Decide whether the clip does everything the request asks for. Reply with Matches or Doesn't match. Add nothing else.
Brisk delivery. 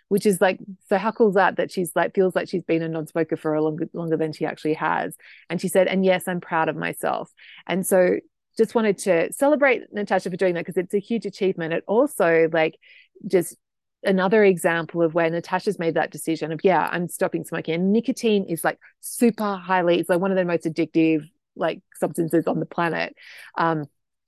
Matches